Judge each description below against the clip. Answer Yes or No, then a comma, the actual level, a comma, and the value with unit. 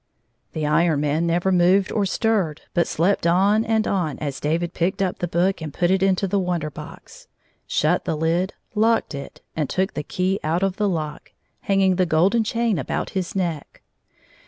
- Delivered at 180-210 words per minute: Yes, average, 185 wpm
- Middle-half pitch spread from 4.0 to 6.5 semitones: No, average, 3.3 semitones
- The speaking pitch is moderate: Yes, medium, 180 Hz